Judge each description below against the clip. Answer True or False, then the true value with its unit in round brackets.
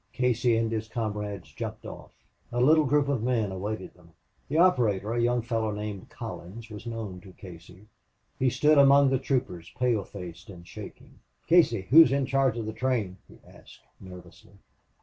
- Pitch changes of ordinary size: True (4.7 semitones)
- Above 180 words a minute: False (170 wpm)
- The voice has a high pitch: False (115 Hz)